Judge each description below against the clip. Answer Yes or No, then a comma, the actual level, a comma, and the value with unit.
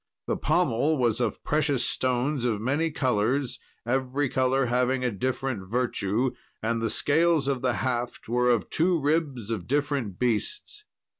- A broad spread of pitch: No, average, 3.2 semitones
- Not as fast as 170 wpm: Yes, average, 150 wpm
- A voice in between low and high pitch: No, low, 130 Hz